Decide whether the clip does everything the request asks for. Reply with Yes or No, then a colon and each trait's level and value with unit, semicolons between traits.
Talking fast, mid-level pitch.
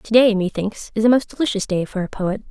No: fast, 240 wpm; high, 210 Hz